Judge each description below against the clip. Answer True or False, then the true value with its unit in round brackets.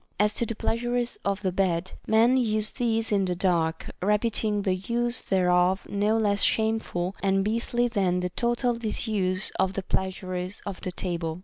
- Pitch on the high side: True (200 Hz)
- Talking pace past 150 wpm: True (170 wpm)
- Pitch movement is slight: False (3.5 semitones)